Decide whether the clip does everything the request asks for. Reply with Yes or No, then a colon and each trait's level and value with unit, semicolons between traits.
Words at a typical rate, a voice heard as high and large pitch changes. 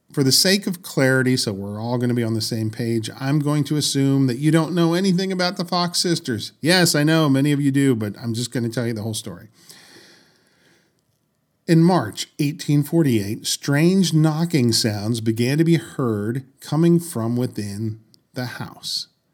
No: average, 185 wpm; low, 135 Hz; wide, 6.1 semitones